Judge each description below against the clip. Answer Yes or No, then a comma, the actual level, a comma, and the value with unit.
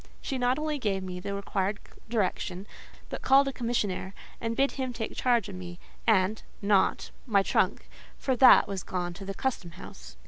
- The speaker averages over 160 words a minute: Yes, average, 175 wpm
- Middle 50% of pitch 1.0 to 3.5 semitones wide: No, average, 4.9 semitones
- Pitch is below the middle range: No, high, 205 Hz